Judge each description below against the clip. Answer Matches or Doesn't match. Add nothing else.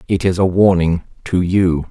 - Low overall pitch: Matches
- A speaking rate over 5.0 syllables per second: Doesn't match